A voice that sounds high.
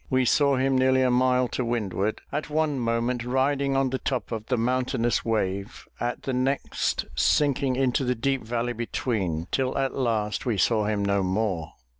No: low, 125 Hz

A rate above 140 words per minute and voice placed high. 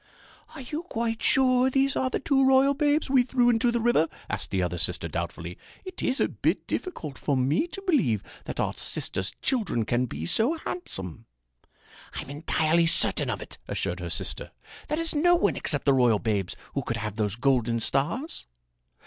No: average, 185 wpm; medium, 170 Hz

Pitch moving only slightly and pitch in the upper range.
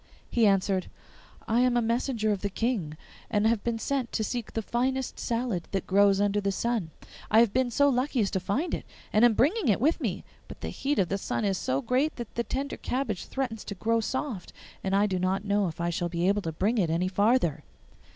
No: average, 4.2 semitones; high, 215 Hz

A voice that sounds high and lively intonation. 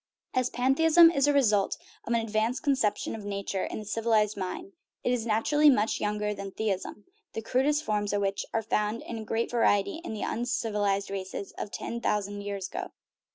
No: high, 220 Hz; average, 3.4 semitones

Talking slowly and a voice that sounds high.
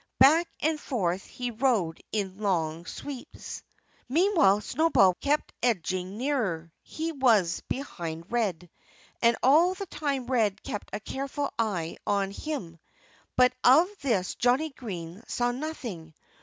Yes: slow, 130 wpm; high, 235 Hz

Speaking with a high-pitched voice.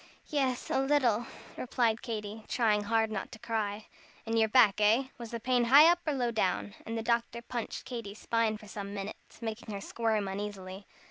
Yes: high, 225 Hz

